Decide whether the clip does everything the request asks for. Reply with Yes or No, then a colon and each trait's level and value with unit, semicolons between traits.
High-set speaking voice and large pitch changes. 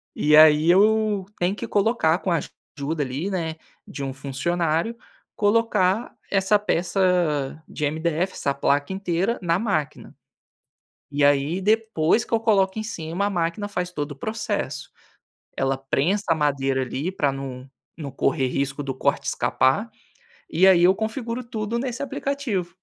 No: medium, 175 Hz; wide, 6.0 semitones